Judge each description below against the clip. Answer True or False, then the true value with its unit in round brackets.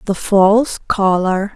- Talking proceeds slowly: True (115 wpm)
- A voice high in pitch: True (200 Hz)